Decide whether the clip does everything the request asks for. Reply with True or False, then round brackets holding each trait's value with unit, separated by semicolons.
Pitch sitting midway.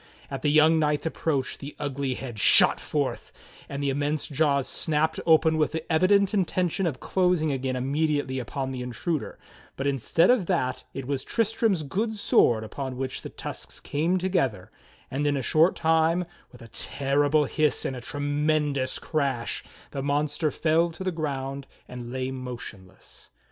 True (145 Hz)